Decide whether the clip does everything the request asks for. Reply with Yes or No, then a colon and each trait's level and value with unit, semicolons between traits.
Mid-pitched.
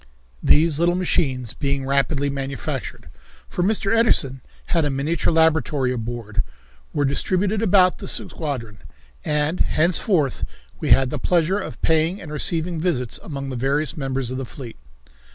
Yes: medium, 150 Hz